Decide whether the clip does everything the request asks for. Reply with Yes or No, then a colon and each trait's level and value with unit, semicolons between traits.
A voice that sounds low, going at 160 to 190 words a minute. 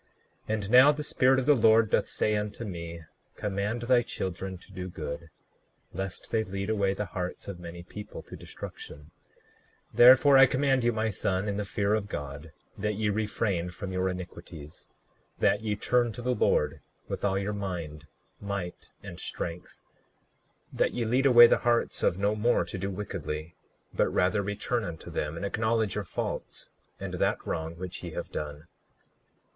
Yes: low, 100 Hz; average, 180 wpm